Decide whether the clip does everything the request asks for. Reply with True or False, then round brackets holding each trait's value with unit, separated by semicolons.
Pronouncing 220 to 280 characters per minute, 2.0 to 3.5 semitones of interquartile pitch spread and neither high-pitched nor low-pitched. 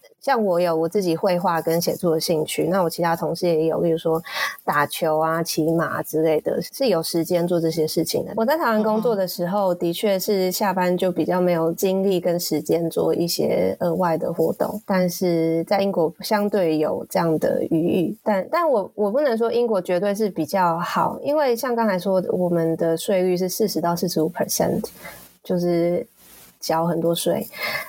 False (290 characters per minute; 3.2 semitones; 175 Hz)